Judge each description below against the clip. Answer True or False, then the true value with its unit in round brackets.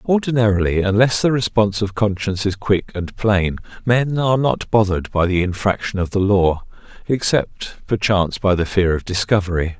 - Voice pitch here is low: True (100 Hz)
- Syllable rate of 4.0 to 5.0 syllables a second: False (5.3 syllables/s)